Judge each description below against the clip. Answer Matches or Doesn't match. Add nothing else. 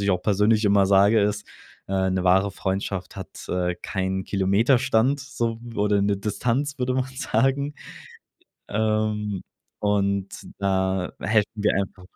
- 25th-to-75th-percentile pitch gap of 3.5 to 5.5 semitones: Doesn't match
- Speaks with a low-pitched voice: Matches